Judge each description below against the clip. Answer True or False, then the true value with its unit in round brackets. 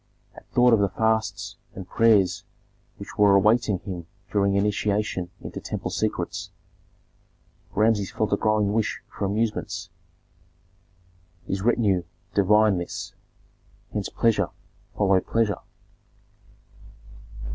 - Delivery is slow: True (105 wpm)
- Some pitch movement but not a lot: False (1.9 semitones)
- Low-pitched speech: True (100 Hz)